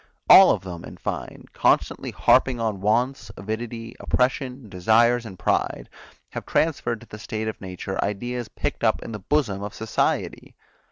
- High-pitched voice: No, low, 110 Hz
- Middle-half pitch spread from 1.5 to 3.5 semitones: Yes, average, 3.2 semitones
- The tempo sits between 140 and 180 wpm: Yes, average, 160 wpm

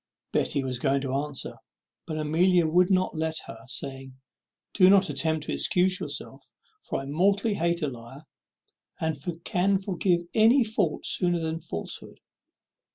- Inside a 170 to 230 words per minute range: No, average, 145 wpm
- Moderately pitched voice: Yes, medium, 165 Hz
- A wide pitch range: No, average, 4.3 semitones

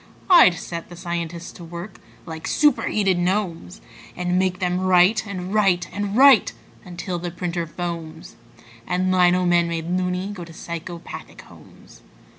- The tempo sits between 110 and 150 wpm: Yes, average, 145 wpm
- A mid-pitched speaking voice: Yes, medium, 180 Hz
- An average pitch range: No, narrow, 1.6 semitones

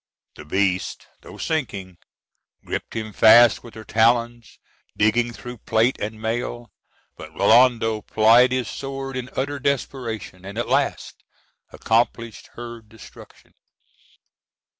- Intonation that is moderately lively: No, narrow, 2.1 semitones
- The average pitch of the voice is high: No, low, 115 Hz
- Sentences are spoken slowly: Yes, slow, 120 wpm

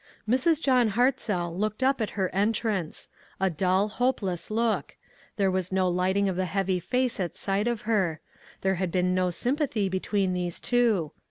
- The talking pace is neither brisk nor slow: Yes, average, 175 wpm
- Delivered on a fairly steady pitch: No, average, 3.9 semitones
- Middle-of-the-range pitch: No, high, 195 Hz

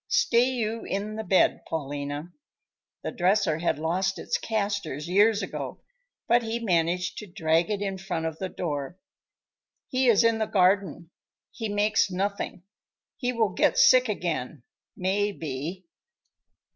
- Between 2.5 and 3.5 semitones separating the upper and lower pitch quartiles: No, average, 4.4 semitones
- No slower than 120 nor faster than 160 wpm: Yes, average, 145 wpm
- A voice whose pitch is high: Yes, high, 195 Hz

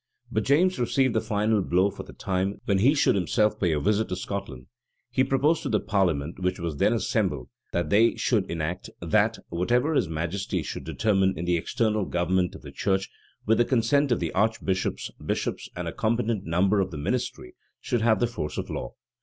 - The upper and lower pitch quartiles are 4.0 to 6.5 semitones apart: Yes, average, 4.3 semitones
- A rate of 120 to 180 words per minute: No, average, 200 wpm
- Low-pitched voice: Yes, low, 100 Hz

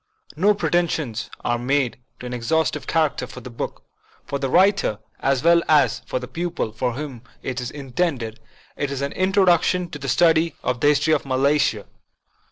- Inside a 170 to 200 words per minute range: Yes, average, 180 wpm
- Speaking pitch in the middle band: Yes, medium, 145 Hz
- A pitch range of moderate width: Yes, average, 4.8 semitones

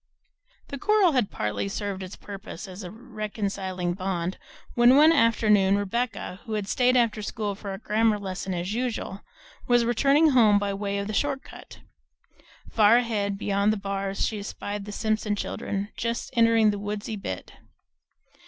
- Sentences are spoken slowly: No, average, 160 wpm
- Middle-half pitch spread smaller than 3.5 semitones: Yes, average, 2.8 semitones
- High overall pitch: Yes, high, 210 Hz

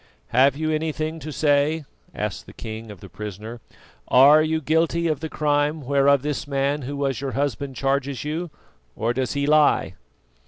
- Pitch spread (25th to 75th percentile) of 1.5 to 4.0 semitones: Yes, narrow, 2.5 semitones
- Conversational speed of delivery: Yes, average, 170 wpm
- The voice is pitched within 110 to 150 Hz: Yes, medium, 140 Hz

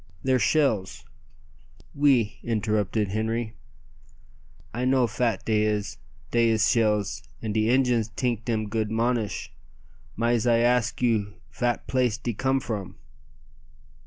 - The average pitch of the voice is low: Yes, low, 115 Hz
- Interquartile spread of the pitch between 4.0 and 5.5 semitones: No, narrow, 2.4 semitones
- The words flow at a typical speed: No, slow, 130 wpm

